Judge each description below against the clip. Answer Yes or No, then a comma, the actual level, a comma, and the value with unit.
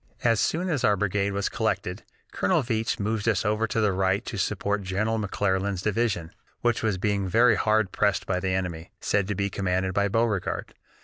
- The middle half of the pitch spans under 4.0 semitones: Yes, average, 2.8 semitones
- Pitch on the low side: Yes, low, 100 Hz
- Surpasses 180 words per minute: Yes, average, 190 wpm